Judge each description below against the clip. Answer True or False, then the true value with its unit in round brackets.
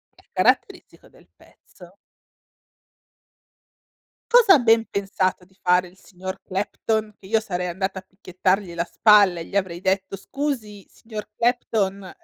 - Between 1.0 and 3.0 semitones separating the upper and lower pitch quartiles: True (2.7 semitones)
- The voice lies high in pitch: True (195 Hz)